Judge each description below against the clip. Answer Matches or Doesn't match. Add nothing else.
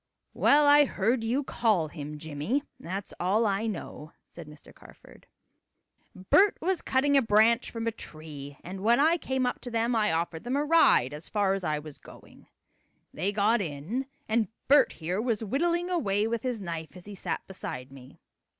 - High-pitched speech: Matches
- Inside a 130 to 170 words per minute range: Doesn't match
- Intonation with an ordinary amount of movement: Doesn't match